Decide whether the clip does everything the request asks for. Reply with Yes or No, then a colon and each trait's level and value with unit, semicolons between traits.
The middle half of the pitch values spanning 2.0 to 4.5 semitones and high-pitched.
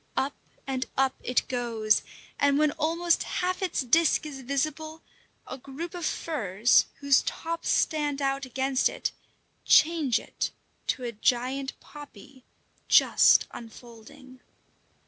Yes: average, 3.6 semitones; very high, 275 Hz